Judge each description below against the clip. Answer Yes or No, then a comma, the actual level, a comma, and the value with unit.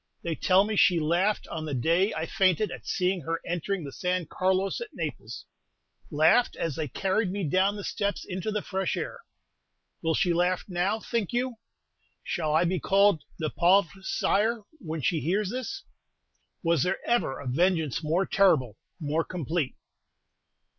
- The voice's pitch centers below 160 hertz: No, medium, 180 Hz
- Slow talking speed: No, average, 165 wpm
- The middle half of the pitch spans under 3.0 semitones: No, average, 3.5 semitones